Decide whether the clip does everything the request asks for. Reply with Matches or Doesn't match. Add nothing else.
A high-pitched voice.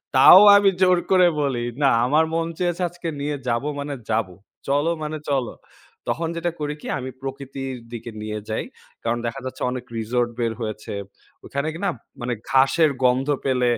Doesn't match